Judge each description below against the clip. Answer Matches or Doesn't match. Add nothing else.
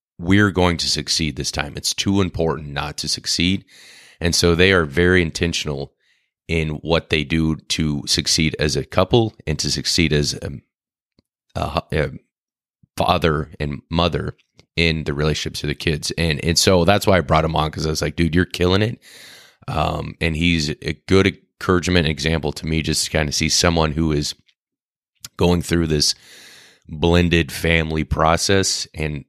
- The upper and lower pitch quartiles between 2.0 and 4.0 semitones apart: Matches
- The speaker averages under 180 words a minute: Matches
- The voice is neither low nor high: Doesn't match